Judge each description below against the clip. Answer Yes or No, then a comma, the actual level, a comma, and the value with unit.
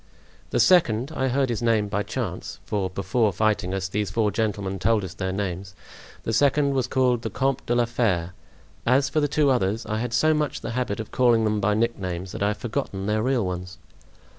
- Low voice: Yes, low, 110 Hz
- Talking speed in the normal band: No, fast, 210 wpm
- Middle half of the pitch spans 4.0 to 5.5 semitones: Yes, average, 4.4 semitones